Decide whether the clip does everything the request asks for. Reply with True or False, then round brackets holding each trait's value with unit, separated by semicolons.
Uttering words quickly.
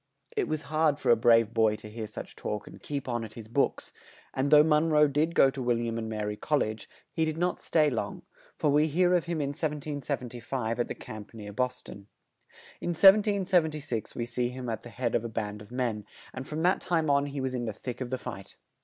True (240 wpm)